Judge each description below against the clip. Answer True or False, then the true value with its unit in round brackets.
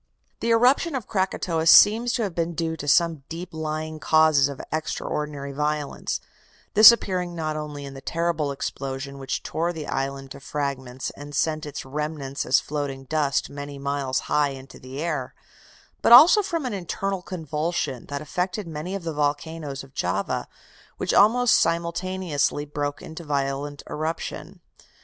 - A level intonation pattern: False (3.5 semitones)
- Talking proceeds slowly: False (155 wpm)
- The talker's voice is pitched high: False (150 Hz)